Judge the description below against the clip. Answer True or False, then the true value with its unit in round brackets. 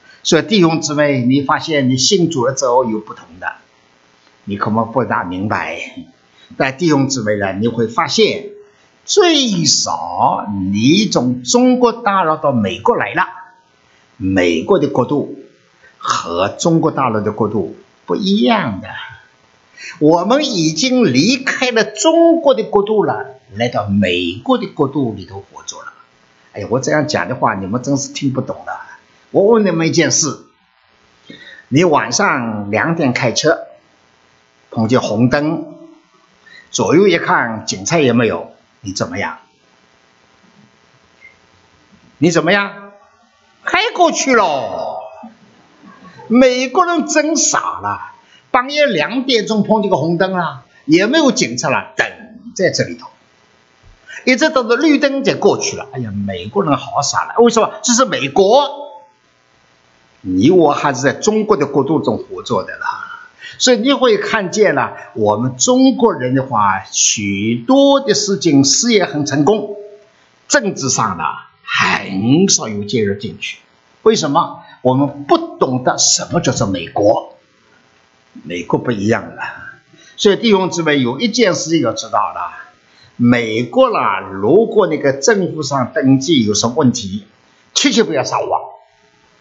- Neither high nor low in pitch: True (150 Hz)